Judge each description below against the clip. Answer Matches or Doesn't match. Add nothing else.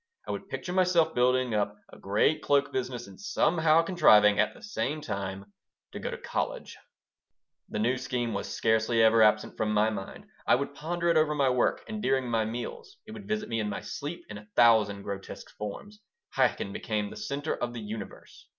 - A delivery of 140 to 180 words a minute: Doesn't match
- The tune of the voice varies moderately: Doesn't match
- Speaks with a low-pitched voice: Matches